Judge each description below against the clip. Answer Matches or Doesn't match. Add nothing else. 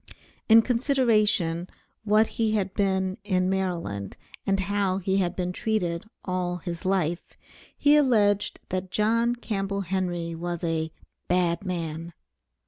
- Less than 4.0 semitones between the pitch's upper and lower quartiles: Matches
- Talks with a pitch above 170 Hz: Matches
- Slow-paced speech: Matches